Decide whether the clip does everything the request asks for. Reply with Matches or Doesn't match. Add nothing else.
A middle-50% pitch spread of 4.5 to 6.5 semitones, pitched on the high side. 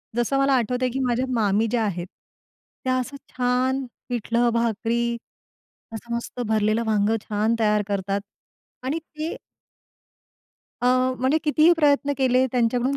Doesn't match